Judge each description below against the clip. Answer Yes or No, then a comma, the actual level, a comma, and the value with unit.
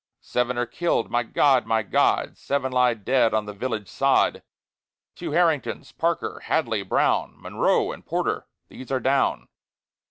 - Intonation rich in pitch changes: No, average, 3.3 semitones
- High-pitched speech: No, low, 125 Hz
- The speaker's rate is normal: Yes, average, 150 wpm